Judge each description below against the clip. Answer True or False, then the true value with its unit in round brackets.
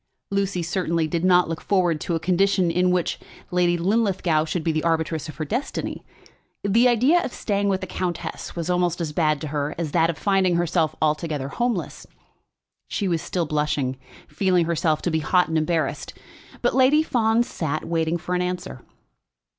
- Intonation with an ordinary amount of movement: True (3.0 semitones)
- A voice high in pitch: False (175 Hz)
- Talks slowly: False (180 wpm)